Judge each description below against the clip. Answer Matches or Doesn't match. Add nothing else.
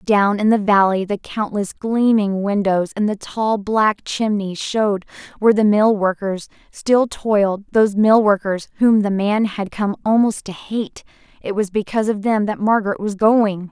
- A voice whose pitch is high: Matches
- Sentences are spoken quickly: Doesn't match